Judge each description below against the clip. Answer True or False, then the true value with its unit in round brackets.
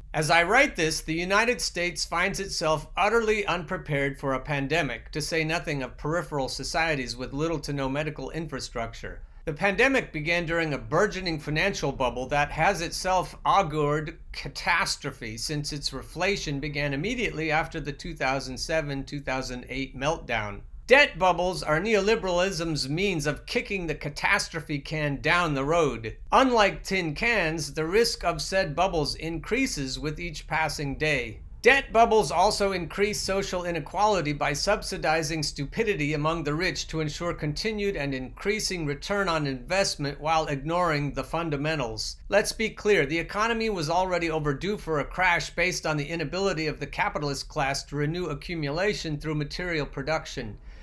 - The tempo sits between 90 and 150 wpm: True (145 wpm)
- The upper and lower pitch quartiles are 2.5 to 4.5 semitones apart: True (4.2 semitones)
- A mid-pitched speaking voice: True (160 Hz)